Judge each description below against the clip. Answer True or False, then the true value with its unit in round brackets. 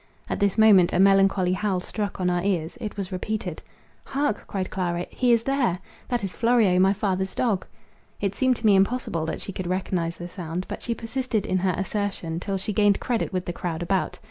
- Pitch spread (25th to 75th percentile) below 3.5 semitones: True (3.1 semitones)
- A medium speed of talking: False (210 wpm)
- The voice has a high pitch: True (195 Hz)